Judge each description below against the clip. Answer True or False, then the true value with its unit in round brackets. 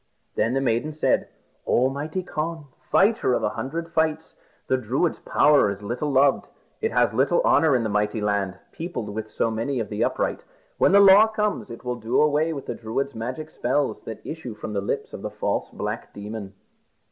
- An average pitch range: False (6.2 semitones)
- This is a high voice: False (130 Hz)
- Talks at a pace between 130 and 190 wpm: False (200 wpm)